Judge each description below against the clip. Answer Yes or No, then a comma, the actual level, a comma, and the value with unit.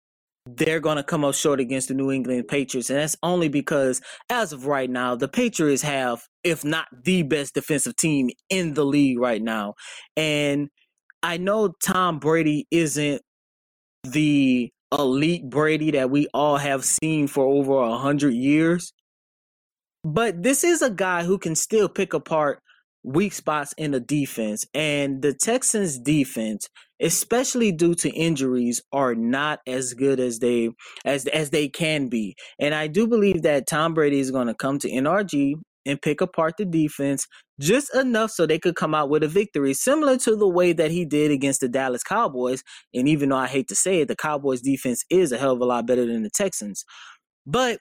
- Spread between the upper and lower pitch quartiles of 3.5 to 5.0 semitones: Yes, average, 4.2 semitones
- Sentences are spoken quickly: No, average, 185 wpm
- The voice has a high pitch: No, medium, 150 Hz